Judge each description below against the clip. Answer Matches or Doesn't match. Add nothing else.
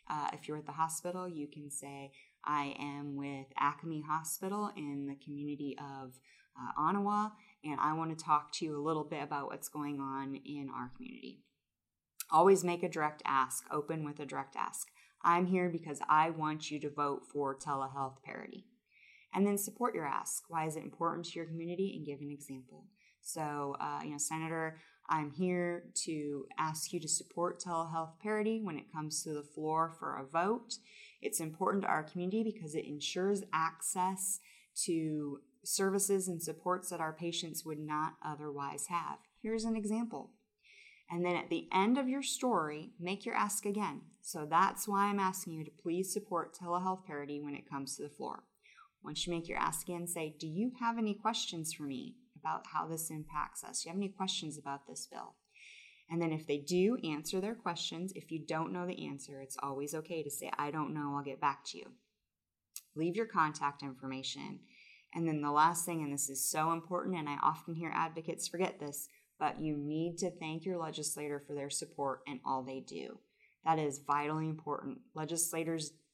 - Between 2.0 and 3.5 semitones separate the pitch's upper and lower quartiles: Doesn't match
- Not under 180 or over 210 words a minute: Matches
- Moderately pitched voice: Matches